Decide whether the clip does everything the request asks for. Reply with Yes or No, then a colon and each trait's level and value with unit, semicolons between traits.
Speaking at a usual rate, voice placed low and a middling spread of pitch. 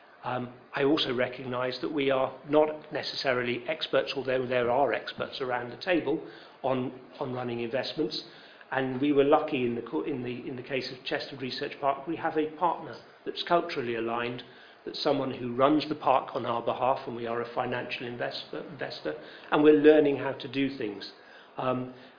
Yes: average, 180 wpm; low, 130 Hz; average, 3.3 semitones